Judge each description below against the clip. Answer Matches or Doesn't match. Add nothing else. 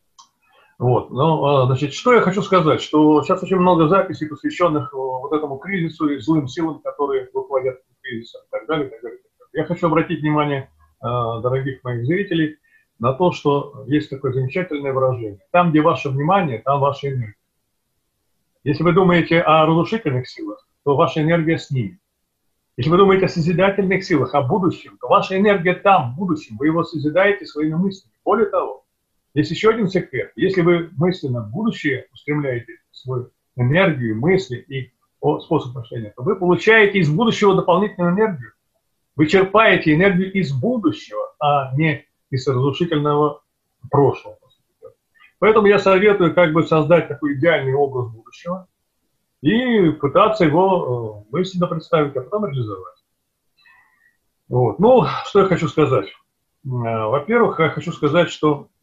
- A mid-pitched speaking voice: Matches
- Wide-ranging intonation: Matches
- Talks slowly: Doesn't match